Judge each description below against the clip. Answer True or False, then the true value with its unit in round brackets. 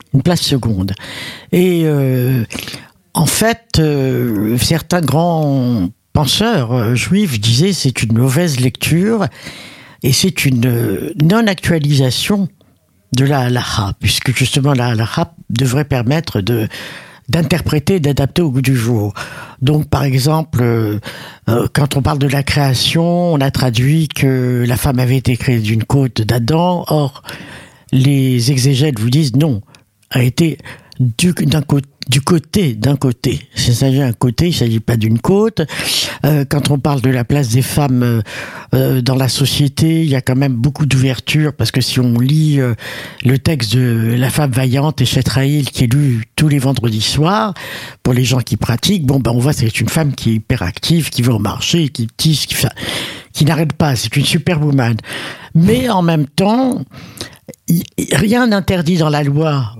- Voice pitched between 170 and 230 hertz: False (135 Hz)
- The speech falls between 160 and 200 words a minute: True (165 wpm)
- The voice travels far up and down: False (4.0 semitones)